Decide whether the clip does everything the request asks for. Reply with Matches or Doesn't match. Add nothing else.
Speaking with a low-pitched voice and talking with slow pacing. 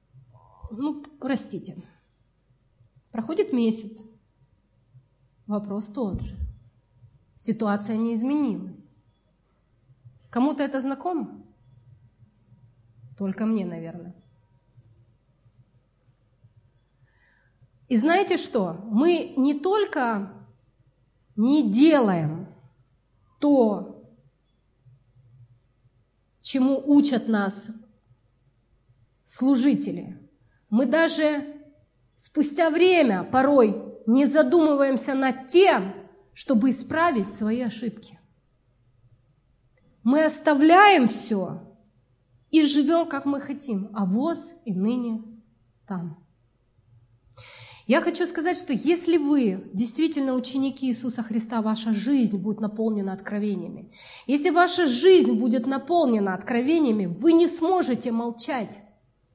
Doesn't match